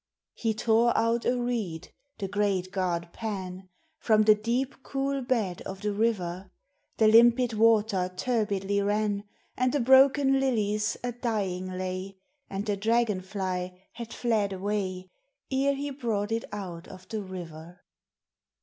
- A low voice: No, high, 210 Hz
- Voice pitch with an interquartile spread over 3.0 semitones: Yes, average, 4.0 semitones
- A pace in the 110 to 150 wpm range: Yes, average, 140 wpm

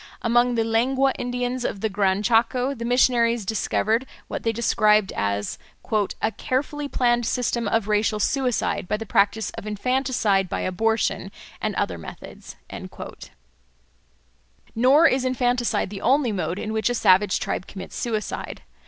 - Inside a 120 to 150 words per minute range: Yes, average, 145 wpm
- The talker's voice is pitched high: Yes, high, 225 Hz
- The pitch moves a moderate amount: Yes, average, 3.0 semitones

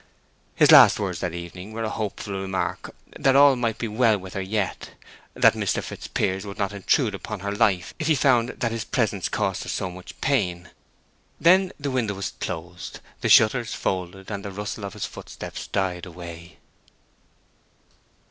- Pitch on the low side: Yes, low, 100 Hz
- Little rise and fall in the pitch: No, average, 3.8 semitones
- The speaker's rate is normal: Yes, average, 175 wpm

